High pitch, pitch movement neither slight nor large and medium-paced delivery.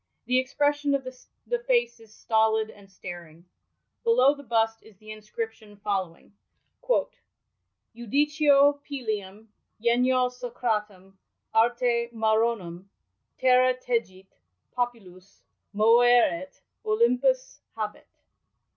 No: high, 230 Hz; average, 3.5 semitones; slow, 95 wpm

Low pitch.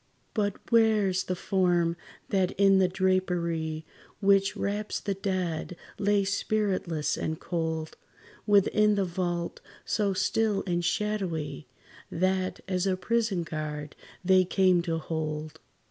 No: medium, 185 Hz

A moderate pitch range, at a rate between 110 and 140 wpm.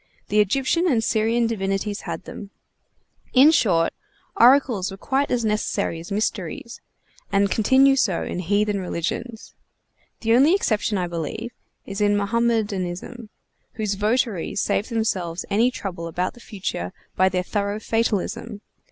Yes: average, 3.6 semitones; slow, 135 wpm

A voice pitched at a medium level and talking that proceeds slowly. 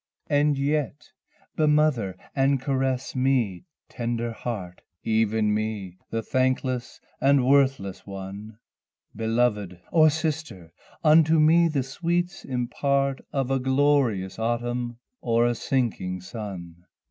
No: low, 125 Hz; slow, 110 wpm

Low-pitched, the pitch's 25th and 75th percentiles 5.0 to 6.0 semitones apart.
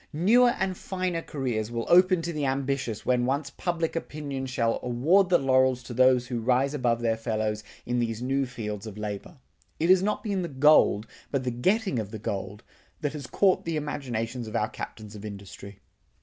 Yes: low, 130 Hz; wide, 5.4 semitones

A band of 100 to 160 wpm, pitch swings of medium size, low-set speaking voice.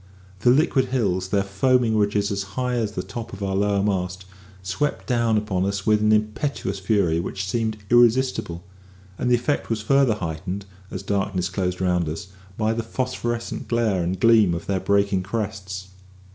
No: average, 170 wpm; average, 3.6 semitones; low, 100 Hz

